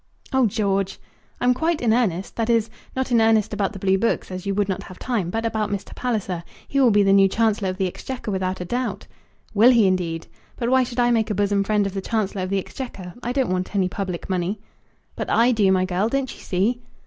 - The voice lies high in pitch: Yes, high, 205 Hz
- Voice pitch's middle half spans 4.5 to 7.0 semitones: No, average, 3.8 semitones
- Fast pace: Yes, fast, 240 wpm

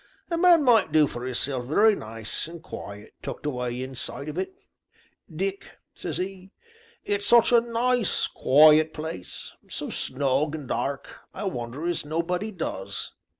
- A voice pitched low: No, medium, 155 Hz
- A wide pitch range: Yes, wide, 7.4 semitones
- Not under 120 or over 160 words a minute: Yes, average, 150 wpm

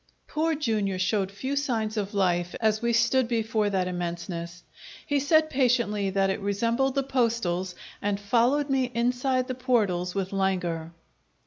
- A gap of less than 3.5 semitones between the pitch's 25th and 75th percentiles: No, average, 4.9 semitones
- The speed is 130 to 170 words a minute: Yes, average, 150 wpm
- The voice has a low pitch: No, high, 220 Hz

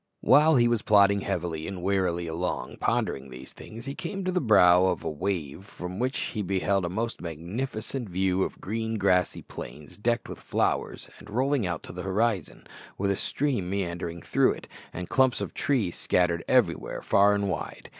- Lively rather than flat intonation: No, average, 4.4 semitones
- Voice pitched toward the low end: Yes, very low, 95 Hz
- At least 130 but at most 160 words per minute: No, average, 185 wpm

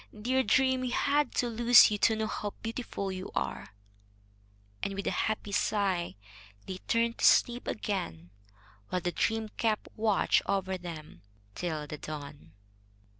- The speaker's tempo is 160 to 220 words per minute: No, average, 150 wpm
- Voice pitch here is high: Yes, high, 205 Hz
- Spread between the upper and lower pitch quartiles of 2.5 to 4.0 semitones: No, average, 4.5 semitones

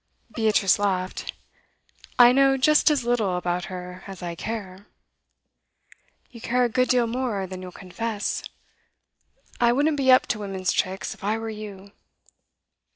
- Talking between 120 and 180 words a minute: Yes, average, 150 wpm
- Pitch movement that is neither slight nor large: Yes, average, 4.6 semitones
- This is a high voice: Yes, high, 215 Hz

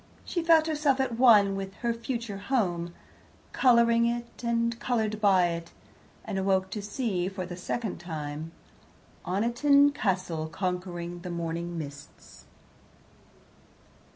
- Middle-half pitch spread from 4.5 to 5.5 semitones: Yes, average, 5.2 semitones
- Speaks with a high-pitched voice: Yes, high, 200 Hz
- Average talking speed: No, slow, 125 wpm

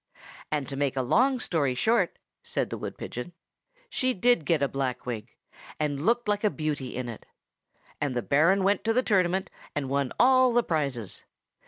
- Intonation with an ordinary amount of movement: No, wide, 7.7 semitones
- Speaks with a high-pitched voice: No, medium, 155 Hz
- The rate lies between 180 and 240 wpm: Yes, average, 185 wpm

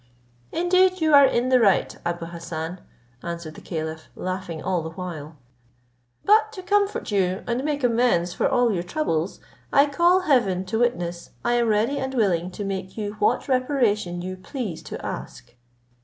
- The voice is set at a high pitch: Yes, high, 205 Hz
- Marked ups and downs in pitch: Yes, wide, 7.4 semitones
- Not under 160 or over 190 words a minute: Yes, average, 170 wpm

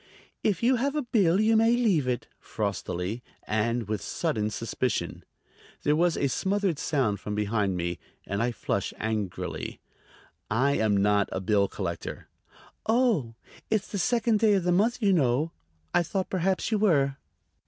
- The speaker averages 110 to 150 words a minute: No, average, 160 wpm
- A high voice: No, medium, 140 Hz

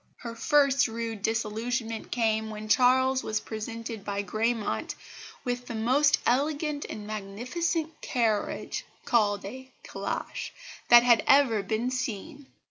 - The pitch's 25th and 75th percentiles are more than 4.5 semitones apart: No, average, 3.2 semitones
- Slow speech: Yes, slow, 125 wpm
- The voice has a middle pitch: No, high, 235 Hz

